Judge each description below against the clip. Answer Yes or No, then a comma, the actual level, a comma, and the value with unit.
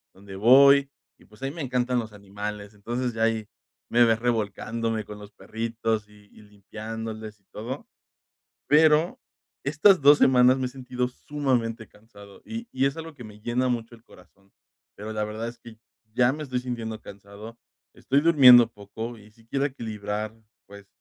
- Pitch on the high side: No, low, 115 Hz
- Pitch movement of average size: Yes, average, 3.4 semitones